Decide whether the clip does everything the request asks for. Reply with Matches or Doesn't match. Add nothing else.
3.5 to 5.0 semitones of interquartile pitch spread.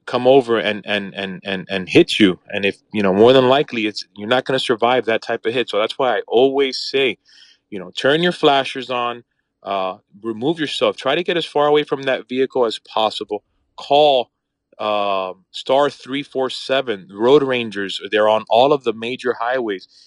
Matches